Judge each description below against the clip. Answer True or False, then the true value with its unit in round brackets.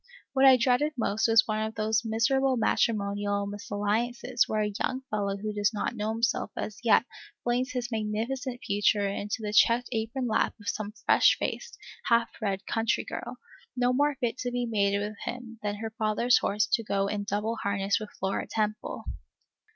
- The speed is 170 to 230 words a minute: True (180 wpm)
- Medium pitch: False (220 Hz)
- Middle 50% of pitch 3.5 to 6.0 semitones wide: False (2.8 semitones)